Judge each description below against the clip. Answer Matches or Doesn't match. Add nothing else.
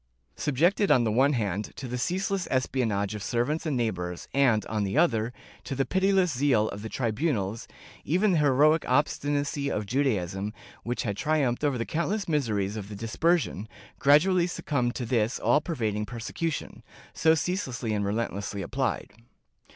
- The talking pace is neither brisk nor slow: Matches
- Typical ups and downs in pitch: Doesn't match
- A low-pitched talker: Matches